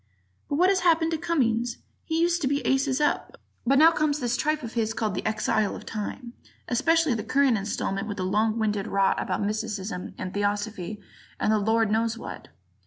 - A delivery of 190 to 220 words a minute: Yes, average, 195 wpm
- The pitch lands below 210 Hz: No, high, 230 Hz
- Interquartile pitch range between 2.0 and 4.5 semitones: No, wide, 5.4 semitones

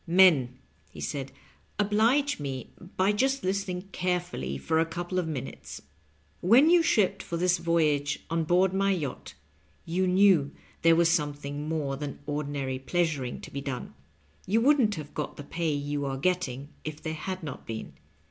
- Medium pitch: Yes, medium, 165 Hz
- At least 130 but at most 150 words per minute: No, average, 165 wpm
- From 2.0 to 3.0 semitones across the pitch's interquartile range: No, average, 4.5 semitones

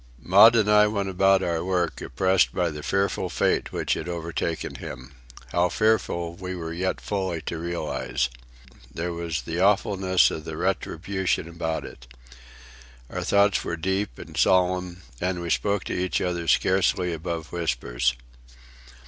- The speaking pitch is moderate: No, very low, 90 Hz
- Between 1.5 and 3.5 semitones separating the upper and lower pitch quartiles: Yes, narrow, 2.5 semitones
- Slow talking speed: No, average, 145 wpm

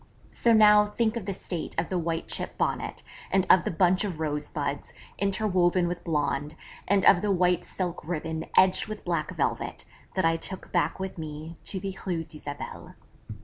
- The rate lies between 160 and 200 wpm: Yes, average, 180 wpm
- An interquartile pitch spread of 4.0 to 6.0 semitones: No, average, 3.1 semitones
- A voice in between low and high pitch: Yes, medium, 180 Hz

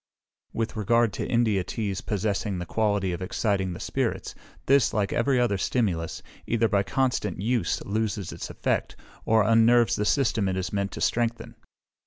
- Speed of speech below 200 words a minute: Yes, average, 165 wpm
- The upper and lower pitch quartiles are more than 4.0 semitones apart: No, average, 3.0 semitones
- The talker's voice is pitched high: No, low, 105 Hz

